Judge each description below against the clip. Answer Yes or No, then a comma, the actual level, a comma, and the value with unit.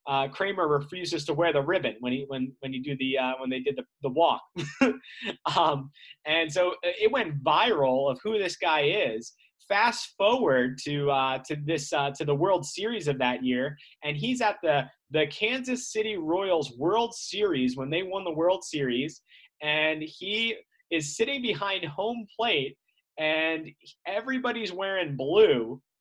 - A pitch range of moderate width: No, wide, 6.9 semitones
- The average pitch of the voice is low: No, medium, 160 Hz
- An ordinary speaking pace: Yes, average, 170 wpm